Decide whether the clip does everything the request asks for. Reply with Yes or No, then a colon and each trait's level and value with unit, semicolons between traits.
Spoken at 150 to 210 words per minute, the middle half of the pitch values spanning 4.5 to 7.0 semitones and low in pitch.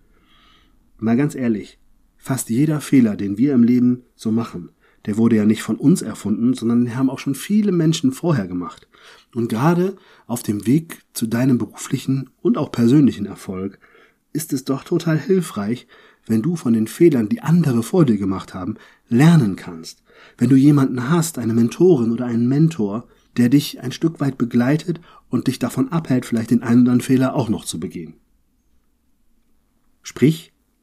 Yes: average, 170 wpm; average, 5.1 semitones; low, 125 Hz